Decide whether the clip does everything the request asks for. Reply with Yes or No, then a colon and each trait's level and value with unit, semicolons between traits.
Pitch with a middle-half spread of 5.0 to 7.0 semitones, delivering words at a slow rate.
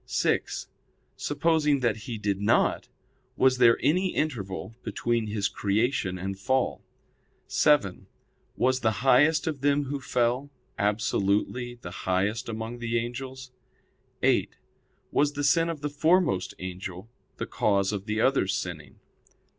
Yes: wide, 5.6 semitones; slow, 130 wpm